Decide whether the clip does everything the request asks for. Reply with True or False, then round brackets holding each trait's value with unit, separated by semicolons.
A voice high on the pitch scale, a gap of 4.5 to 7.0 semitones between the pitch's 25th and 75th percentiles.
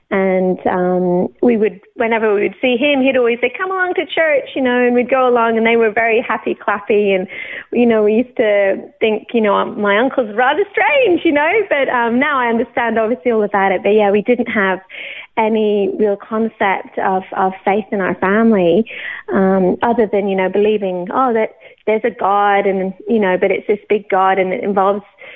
False (220 Hz; 4.0 semitones)